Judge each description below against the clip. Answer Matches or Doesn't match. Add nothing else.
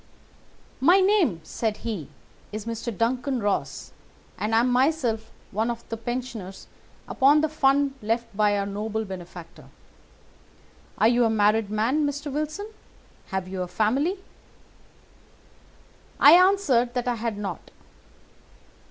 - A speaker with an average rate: Doesn't match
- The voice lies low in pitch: Doesn't match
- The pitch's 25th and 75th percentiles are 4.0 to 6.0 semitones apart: Matches